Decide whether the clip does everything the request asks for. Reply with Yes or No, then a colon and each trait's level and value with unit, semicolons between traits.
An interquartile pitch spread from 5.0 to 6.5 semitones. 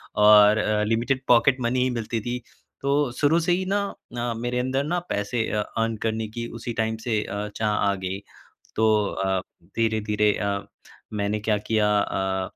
No: average, 2.7 semitones